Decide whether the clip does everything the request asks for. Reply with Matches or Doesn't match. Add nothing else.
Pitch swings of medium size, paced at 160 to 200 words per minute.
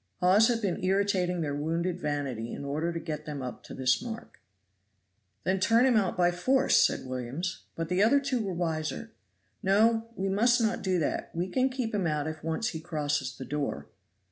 Doesn't match